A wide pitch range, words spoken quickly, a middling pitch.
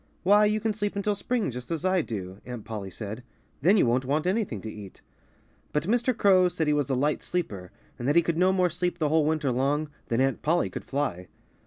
Yes: wide, 7.0 semitones; fast, 230 wpm; medium, 155 Hz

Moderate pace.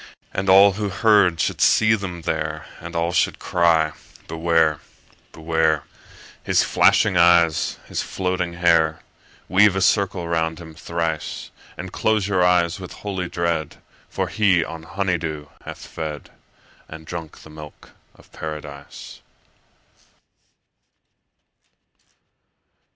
No: slow, 125 wpm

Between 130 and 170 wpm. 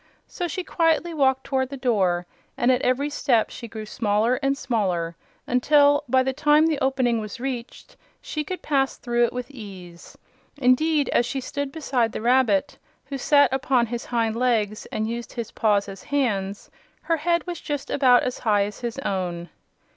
No: average, 180 wpm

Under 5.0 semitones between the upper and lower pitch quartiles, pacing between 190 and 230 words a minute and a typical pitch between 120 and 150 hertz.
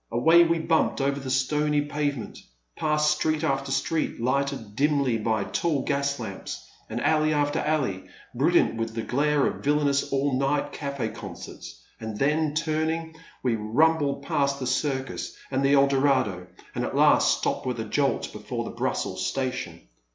No: average, 2.9 semitones; average, 160 wpm; medium, 140 Hz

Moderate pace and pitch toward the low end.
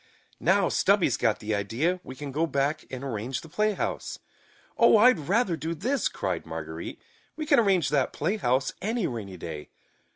No: average, 165 wpm; medium, 155 Hz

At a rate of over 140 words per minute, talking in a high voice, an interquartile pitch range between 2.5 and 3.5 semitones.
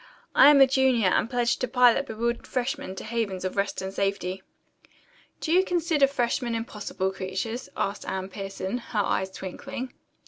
No: average, 165 wpm; high, 230 Hz; wide, 5.4 semitones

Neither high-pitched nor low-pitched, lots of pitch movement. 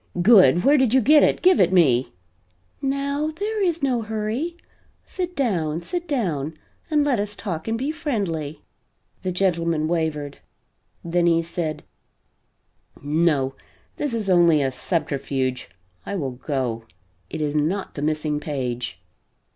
Yes: medium, 175 Hz; wide, 9.0 semitones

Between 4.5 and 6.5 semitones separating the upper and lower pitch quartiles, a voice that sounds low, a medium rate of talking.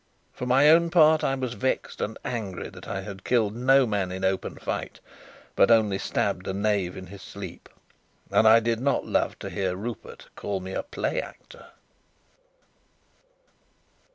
Yes: average, 4.9 semitones; low, 110 Hz; average, 165 wpm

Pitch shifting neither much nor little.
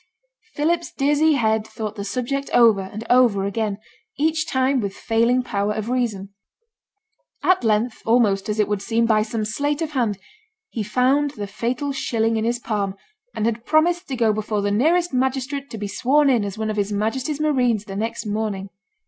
Yes: average, 4.4 semitones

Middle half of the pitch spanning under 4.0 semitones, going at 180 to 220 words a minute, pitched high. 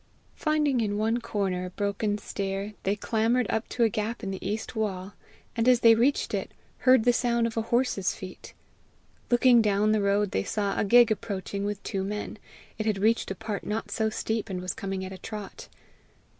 Yes: narrow, 2.6 semitones; average, 200 wpm; high, 215 Hz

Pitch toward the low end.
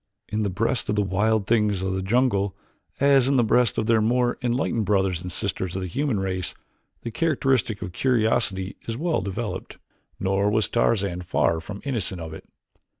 Yes: low, 105 Hz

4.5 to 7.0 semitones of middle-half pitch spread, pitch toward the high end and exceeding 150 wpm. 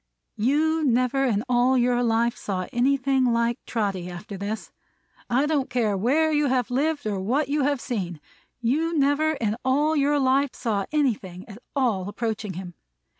Yes: average, 4.8 semitones; high, 245 Hz; average, 165 wpm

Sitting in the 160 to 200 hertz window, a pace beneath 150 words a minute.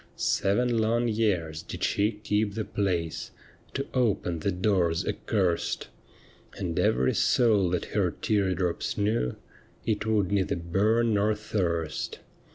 No: low, 100 Hz; slow, 135 wpm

